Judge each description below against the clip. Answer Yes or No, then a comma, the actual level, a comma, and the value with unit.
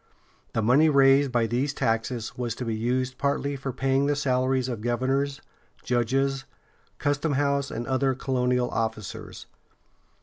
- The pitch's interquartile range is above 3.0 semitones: No, narrow, 2.4 semitones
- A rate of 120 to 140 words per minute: Yes, slow, 135 wpm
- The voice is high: No, low, 130 Hz